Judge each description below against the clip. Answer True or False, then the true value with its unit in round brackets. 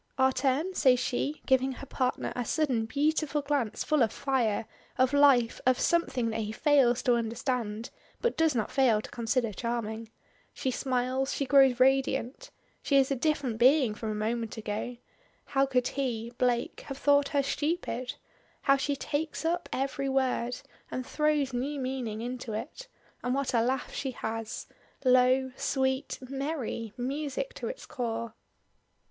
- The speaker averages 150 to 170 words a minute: True (160 wpm)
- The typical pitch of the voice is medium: False (260 Hz)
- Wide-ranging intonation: False (2.9 semitones)